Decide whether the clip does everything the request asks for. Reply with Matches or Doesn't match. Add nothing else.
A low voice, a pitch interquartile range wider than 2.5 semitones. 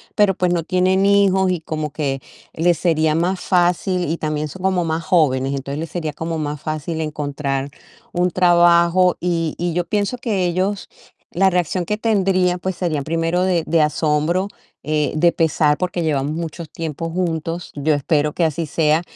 Doesn't match